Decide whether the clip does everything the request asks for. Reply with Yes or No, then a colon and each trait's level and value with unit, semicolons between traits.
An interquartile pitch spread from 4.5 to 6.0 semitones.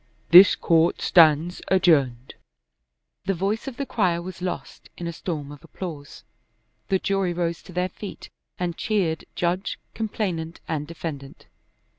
No: average, 2.7 semitones